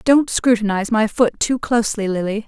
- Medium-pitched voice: No, high, 220 Hz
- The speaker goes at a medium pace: Yes, average, 170 wpm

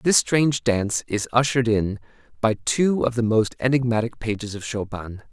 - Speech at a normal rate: Yes, average, 170 wpm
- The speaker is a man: Yes, male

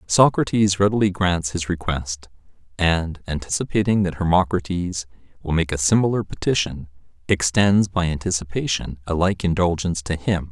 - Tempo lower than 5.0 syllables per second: No, 5.1 syllables/s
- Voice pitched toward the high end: No, very low, 90 Hz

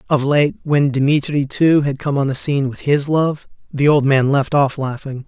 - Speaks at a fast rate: Yes, fast, 215 wpm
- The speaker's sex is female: No, male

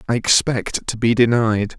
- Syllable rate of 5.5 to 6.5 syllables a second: No, 4.4 syllables/s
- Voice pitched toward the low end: Yes, low, 115 Hz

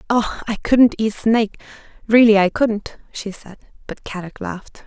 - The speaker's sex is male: No, female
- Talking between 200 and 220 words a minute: No, average, 160 wpm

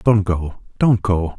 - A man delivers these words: Yes, male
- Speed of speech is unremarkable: Yes, average, 175 wpm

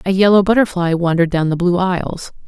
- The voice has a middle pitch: Yes, medium, 180 Hz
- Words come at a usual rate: Yes, average, 195 wpm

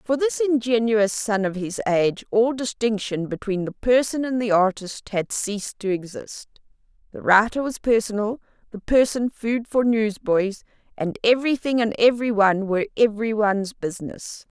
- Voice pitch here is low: No, high, 220 Hz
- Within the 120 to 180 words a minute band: Yes, average, 150 wpm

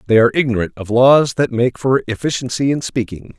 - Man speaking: Yes, male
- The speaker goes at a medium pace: Yes, average, 195 wpm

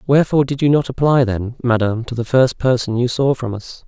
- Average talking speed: No, fast, 230 wpm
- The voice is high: No, low, 125 Hz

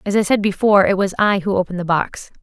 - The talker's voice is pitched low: No, high, 195 Hz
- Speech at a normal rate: No, fast, 270 wpm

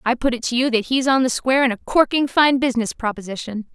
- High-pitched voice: Yes, very high, 250 Hz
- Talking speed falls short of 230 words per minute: No, fast, 255 wpm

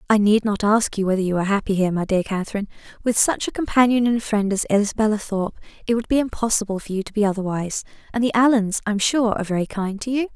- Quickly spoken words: Yes, fast, 245 wpm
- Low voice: No, high, 210 Hz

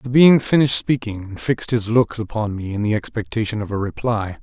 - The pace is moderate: No, fast, 215 wpm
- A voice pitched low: Yes, low, 115 Hz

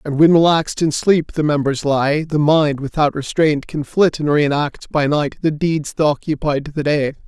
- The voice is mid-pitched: Yes, medium, 150 Hz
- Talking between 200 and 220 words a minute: Yes, fast, 205 wpm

